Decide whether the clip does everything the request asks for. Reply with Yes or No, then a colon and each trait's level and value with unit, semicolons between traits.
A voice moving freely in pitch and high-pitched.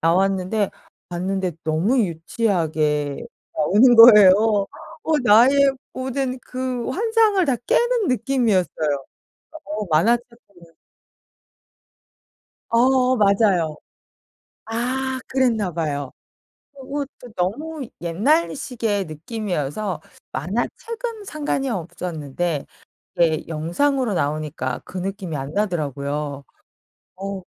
Yes: wide, 7.8 semitones; high, 200 Hz